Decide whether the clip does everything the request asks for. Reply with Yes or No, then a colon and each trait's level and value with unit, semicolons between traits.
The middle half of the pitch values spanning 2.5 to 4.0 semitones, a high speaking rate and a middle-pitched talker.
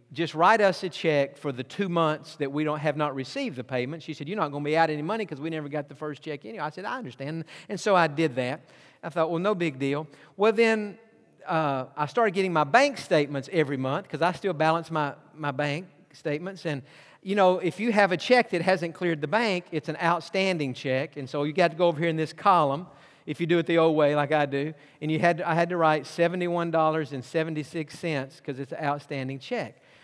Yes: average, 3.0 semitones; fast, 240 wpm; medium, 160 Hz